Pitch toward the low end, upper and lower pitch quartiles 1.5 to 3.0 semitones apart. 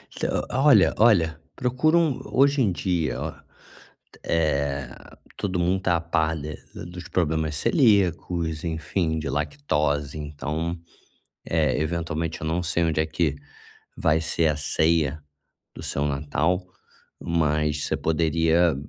Yes: very low, 80 Hz; narrow, 2.5 semitones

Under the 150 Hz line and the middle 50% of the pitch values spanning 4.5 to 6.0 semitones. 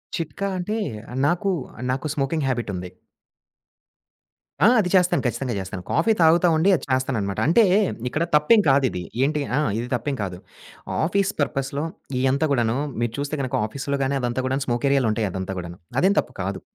Yes: low, 135 Hz; average, 5.2 semitones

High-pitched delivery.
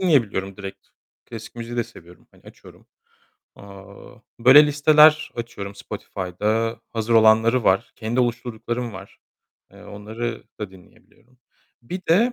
No: low, 115 Hz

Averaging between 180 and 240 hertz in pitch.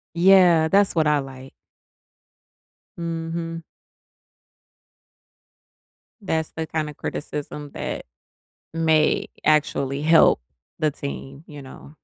No: medium, 155 Hz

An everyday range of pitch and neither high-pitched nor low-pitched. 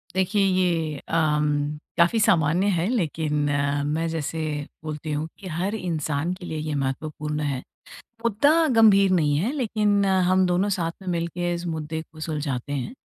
Yes: average, 3.6 semitones; medium, 170 Hz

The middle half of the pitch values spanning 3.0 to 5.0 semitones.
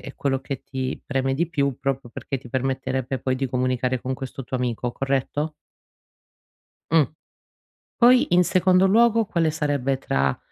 Yes: average, 3.5 semitones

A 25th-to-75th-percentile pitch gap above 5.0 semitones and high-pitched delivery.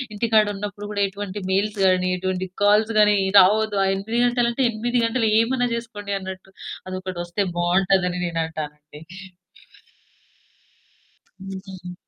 No: average, 2.8 semitones; high, 195 Hz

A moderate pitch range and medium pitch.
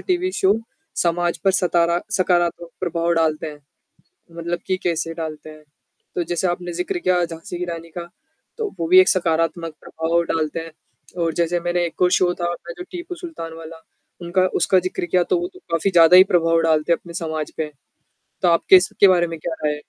No: narrow, 1.6 semitones; medium, 170 Hz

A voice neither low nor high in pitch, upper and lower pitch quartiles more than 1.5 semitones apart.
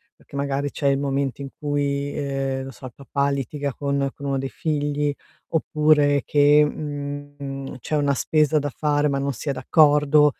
No: medium, 145 Hz; narrow, 1.1 semitones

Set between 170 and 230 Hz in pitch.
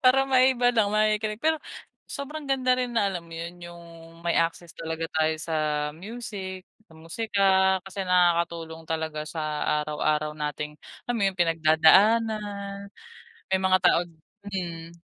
Yes: medium, 185 Hz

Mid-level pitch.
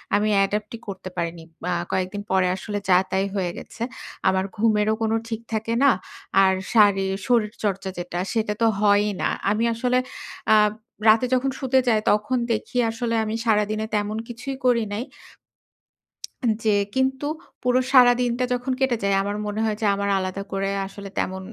No: high, 215 Hz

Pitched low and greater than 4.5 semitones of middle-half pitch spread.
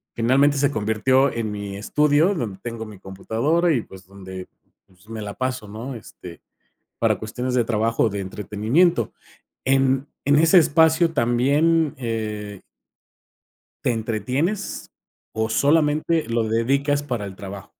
Yes: low, 120 Hz; average, 5.2 semitones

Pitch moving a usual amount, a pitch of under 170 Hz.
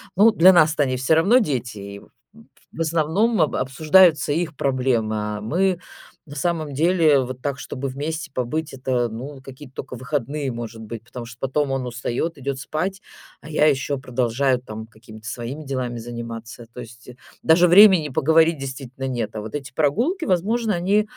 Yes: average, 4.8 semitones; medium, 140 Hz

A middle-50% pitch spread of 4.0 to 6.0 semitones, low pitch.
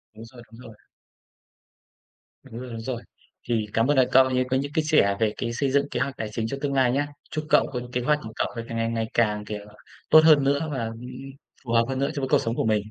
No: average, 3.5 semitones; low, 125 Hz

